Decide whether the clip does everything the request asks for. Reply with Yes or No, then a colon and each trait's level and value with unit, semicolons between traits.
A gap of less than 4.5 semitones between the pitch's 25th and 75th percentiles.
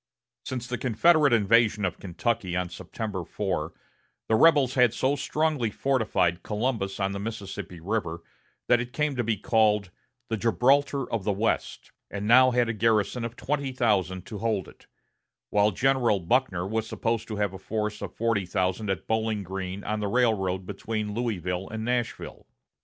Yes: average, 3.8 semitones